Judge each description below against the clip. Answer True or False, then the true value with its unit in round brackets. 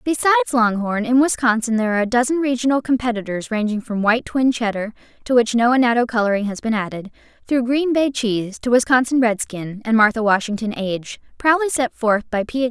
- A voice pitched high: True (235 Hz)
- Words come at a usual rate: True (190 wpm)